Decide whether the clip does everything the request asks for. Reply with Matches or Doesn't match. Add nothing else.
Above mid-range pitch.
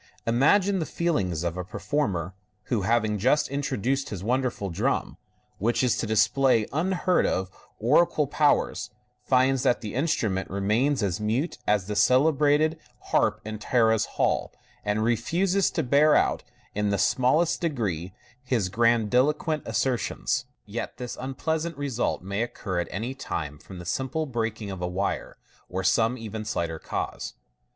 Doesn't match